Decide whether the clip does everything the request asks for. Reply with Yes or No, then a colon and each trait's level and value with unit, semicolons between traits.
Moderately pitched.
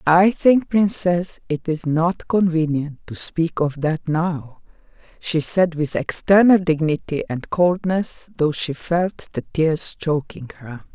Yes: medium, 165 Hz